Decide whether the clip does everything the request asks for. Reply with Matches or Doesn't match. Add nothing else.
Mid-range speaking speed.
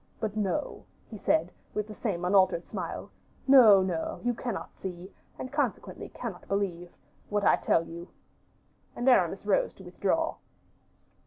Matches